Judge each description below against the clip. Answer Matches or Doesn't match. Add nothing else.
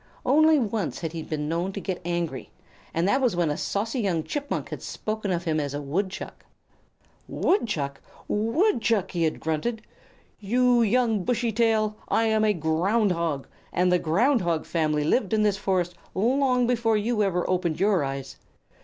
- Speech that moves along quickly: Doesn't match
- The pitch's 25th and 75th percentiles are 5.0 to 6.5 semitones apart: Matches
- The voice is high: Matches